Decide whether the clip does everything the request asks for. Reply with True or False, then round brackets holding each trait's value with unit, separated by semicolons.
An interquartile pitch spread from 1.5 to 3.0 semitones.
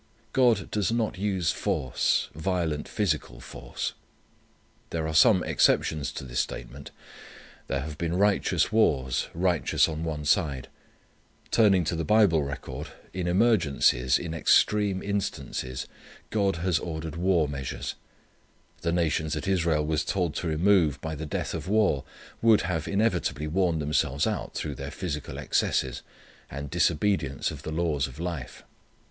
False (4.3 semitones)